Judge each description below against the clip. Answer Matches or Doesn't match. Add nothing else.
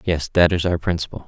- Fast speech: Matches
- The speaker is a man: Matches